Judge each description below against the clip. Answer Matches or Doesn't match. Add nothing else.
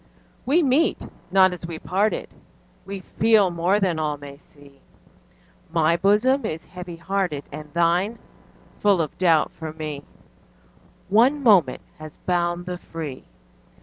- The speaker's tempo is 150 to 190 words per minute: Doesn't match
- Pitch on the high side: Doesn't match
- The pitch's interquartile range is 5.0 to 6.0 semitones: Doesn't match